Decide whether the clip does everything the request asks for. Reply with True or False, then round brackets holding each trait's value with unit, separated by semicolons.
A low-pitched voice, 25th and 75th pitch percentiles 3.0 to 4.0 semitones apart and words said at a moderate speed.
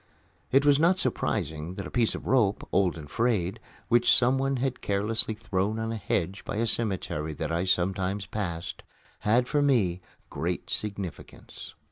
False (105 Hz; 4.7 semitones; 160 wpm)